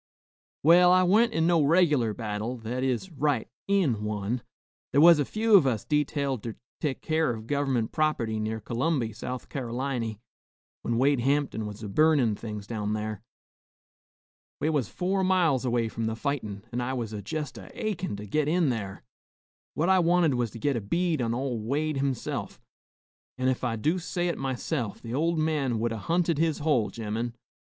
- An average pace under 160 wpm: No, average, 180 wpm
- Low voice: Yes, low, 130 Hz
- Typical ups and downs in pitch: No, wide, 5.7 semitones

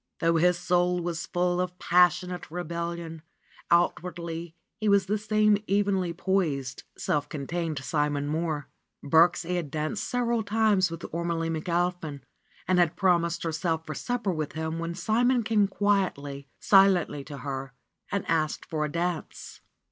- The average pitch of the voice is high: No, medium, 170 Hz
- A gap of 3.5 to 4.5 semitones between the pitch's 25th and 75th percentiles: No, average, 2.9 semitones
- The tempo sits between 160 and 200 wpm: No, average, 150 wpm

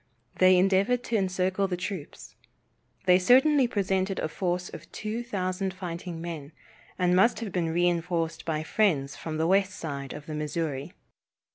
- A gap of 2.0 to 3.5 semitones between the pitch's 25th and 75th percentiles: Yes, average, 3.0 semitones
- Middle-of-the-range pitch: Yes, medium, 180 Hz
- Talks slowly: No, average, 155 wpm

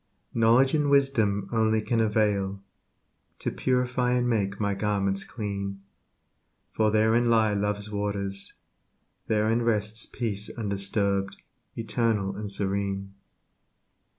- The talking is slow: Yes, slow, 105 wpm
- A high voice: No, low, 105 Hz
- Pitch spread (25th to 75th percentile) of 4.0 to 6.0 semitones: No, narrow, 2.5 semitones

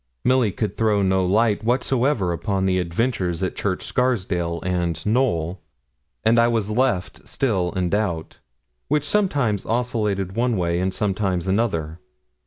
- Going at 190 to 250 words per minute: No, average, 140 wpm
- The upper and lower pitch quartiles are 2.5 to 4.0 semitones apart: No, average, 4.6 semitones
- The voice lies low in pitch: Yes, low, 100 Hz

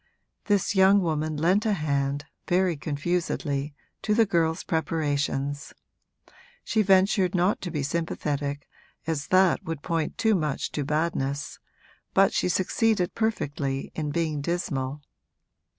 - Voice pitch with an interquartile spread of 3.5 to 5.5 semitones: Yes, average, 4.4 semitones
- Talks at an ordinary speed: No, slow, 125 wpm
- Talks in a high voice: No, medium, 160 Hz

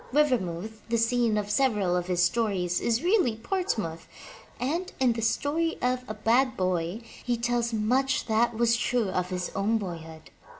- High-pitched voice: Yes, high, 225 Hz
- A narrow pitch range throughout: No, average, 5.0 semitones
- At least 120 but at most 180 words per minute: Yes, average, 165 wpm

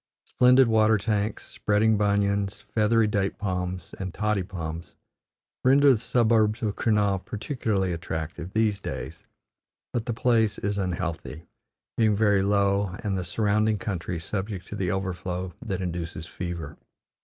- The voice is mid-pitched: No, low, 100 Hz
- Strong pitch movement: No, average, 3.1 semitones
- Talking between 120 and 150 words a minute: Yes, slow, 135 wpm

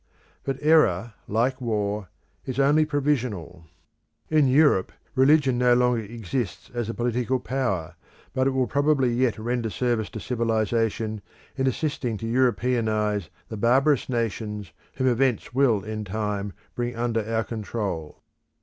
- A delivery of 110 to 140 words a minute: Yes, slow, 135 wpm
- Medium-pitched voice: No, low, 120 Hz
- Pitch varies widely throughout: No, average, 3.4 semitones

